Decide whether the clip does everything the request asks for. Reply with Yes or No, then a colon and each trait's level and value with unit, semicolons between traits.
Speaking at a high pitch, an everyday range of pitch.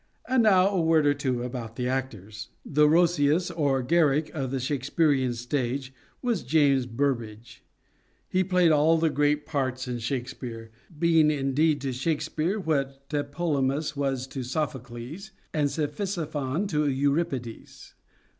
No: medium, 145 Hz; average, 3.5 semitones